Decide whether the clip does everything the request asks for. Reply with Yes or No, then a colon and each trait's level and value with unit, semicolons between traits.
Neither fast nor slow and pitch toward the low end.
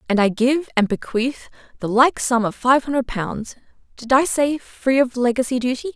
No: average, 180 wpm; very high, 250 Hz